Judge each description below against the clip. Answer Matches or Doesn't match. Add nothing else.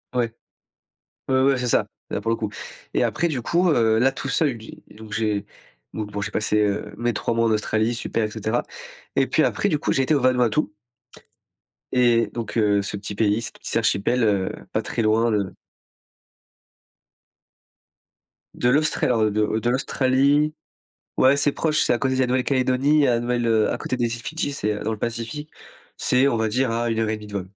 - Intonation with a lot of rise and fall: Doesn't match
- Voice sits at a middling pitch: Doesn't match